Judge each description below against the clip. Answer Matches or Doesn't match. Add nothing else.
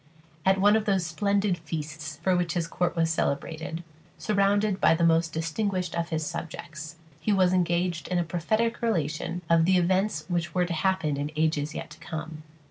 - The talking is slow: Doesn't match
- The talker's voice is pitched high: Doesn't match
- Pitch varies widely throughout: Doesn't match